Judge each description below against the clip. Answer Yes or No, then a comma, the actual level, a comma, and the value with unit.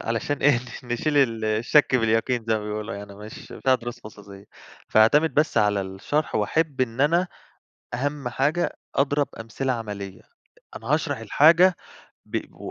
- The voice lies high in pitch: No, low, 120 Hz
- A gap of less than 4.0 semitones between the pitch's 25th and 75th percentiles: No, average, 5.2 semitones